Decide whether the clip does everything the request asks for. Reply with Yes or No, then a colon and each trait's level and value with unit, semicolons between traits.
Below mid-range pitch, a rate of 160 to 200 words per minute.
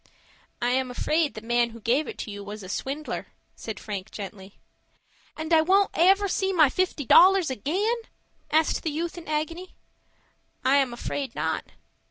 No: very high, 285 Hz; average, 170 wpm